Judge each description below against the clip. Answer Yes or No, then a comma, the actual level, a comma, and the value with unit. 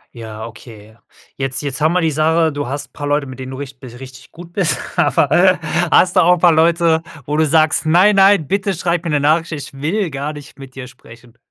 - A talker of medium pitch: Yes, medium, 150 Hz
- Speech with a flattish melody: No, average, 4.2 semitones